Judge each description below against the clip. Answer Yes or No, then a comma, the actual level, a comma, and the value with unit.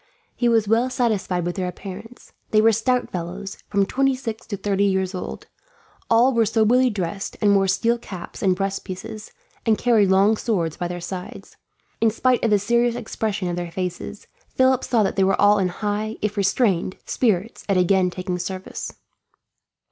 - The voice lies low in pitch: No, high, 205 Hz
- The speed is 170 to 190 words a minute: Yes, average, 180 wpm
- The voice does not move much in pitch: No, average, 3.4 semitones